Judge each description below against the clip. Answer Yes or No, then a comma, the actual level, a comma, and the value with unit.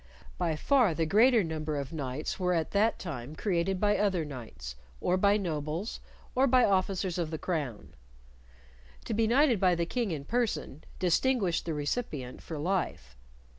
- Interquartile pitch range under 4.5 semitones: No, average, 5.3 semitones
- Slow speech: No, average, 165 wpm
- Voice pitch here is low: No, medium, 175 Hz